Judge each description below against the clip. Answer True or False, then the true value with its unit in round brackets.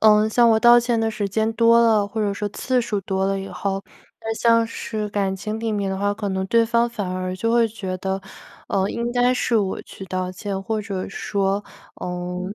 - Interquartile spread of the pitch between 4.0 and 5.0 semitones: False (2.9 semitones)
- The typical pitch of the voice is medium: False (210 Hz)